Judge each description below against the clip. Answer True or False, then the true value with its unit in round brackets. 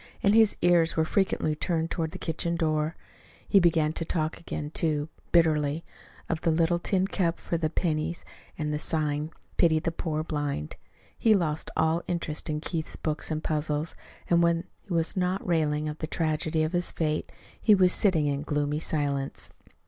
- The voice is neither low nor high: True (160 Hz)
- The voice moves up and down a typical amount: False (2.0 semitones)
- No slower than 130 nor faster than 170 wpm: False (180 wpm)